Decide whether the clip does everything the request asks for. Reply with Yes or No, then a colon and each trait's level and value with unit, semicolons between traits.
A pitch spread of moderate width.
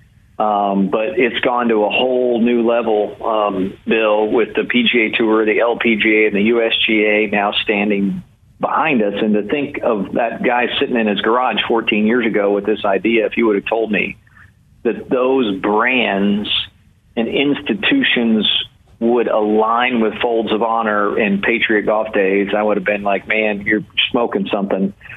No: narrow, 2.2 semitones